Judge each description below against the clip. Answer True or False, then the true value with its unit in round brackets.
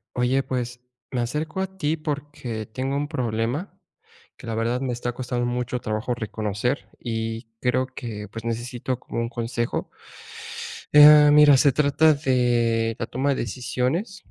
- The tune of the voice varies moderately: True (3.5 semitones)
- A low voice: True (125 Hz)